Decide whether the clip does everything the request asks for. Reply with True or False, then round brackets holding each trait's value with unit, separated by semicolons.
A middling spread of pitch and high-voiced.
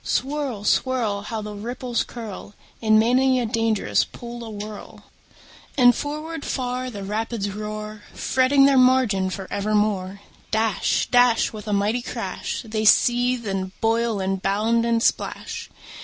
True (3.0 semitones; 225 Hz)